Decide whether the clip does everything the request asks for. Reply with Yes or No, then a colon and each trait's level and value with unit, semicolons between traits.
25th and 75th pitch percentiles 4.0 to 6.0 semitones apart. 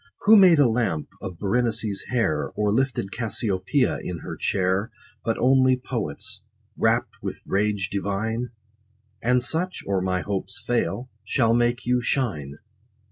Yes: average, 4.3 semitones